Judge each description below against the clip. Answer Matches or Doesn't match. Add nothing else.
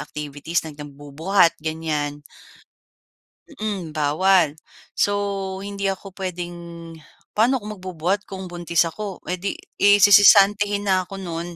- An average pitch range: Matches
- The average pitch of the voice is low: Doesn't match